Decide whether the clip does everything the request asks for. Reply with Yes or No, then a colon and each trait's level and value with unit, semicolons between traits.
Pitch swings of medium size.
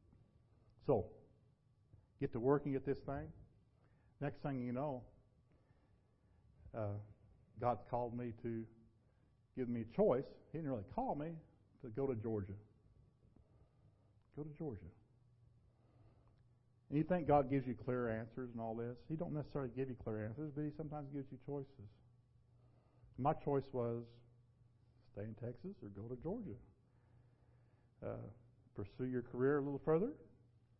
Yes: average, 3.0 semitones